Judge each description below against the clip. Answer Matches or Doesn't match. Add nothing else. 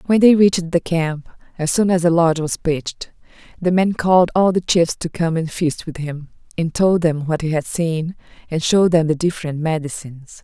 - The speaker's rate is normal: Doesn't match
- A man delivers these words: Doesn't match